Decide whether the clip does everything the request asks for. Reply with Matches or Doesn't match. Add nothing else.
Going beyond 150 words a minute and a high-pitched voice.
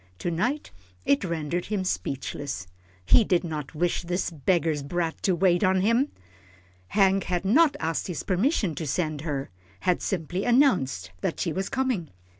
Doesn't match